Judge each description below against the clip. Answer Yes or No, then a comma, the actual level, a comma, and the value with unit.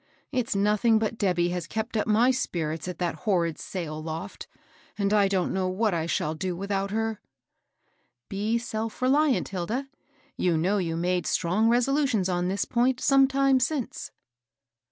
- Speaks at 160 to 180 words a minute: Yes, average, 165 wpm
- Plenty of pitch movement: No, average, 4.8 semitones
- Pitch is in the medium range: No, high, 200 Hz